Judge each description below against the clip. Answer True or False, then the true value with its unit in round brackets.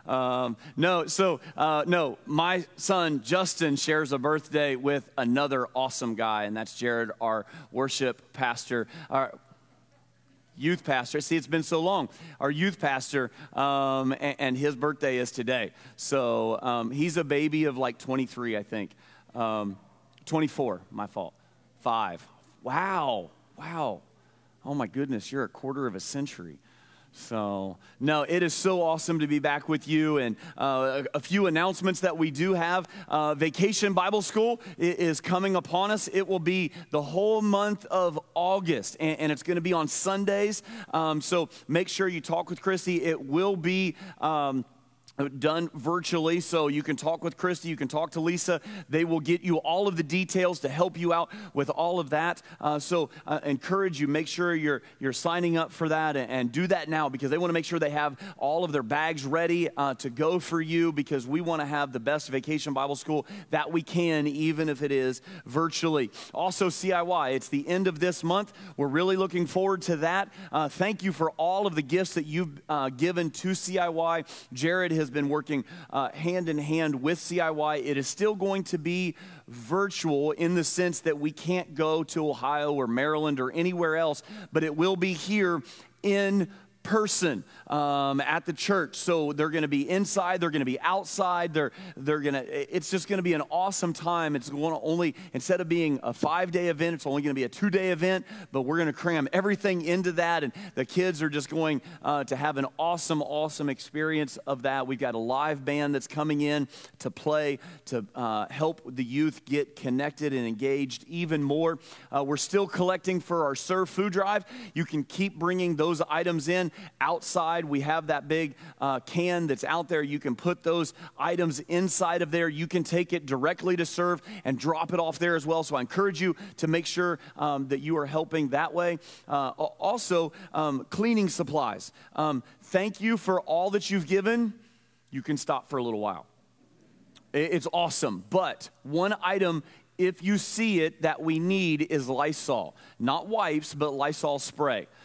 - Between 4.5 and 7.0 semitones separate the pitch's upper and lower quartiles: False (3.7 semitones)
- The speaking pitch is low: False (160 Hz)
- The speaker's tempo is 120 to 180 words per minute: False (190 wpm)